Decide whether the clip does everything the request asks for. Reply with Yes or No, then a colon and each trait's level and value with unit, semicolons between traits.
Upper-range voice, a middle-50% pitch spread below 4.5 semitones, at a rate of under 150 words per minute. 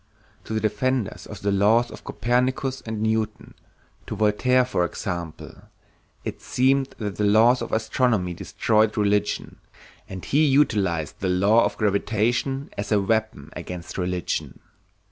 No: low, 110 Hz; average, 3.5 semitones; average, 140 wpm